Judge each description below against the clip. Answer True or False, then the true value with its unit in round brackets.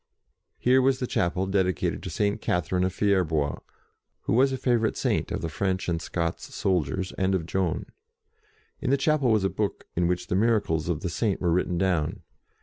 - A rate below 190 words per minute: False (195 wpm)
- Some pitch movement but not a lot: True (3.8 semitones)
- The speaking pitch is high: False (95 Hz)